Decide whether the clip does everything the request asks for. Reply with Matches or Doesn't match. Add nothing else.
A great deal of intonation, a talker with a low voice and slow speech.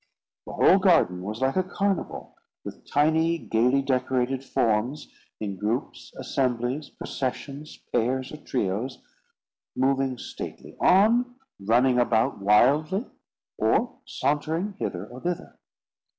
Doesn't match